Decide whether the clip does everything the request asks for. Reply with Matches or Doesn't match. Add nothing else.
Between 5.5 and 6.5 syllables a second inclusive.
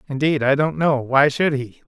Doesn't match